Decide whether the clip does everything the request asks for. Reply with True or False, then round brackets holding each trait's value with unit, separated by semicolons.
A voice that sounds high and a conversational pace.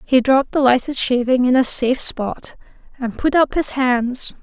True (255 Hz; 190 wpm)